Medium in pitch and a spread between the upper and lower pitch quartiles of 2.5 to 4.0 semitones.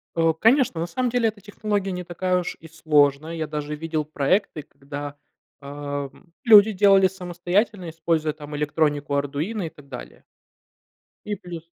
No: medium, 165 Hz; average, 4.6 semitones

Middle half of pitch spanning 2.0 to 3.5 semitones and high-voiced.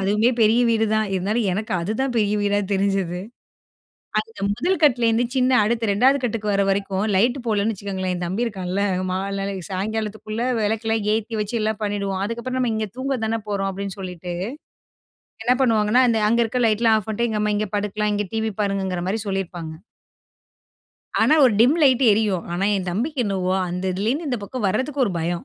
Yes: average, 2.9 semitones; high, 210 Hz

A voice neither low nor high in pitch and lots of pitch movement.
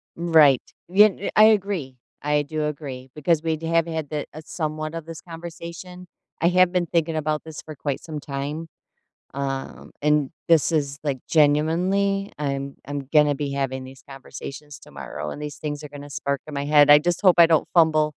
No: medium, 150 Hz; average, 2.7 semitones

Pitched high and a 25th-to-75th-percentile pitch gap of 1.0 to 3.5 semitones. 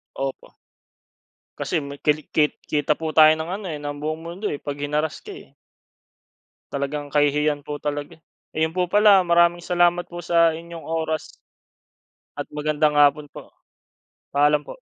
No: medium, 155 Hz; narrow, 2.6 semitones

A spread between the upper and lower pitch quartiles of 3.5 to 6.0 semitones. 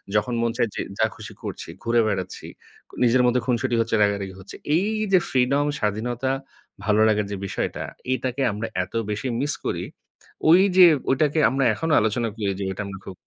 Yes: average, 3.9 semitones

